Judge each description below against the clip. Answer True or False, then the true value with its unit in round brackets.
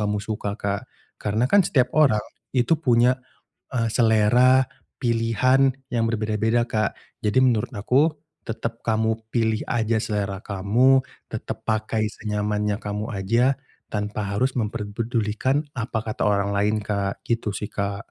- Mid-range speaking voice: False (110 Hz)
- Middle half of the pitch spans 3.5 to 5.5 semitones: False (2.6 semitones)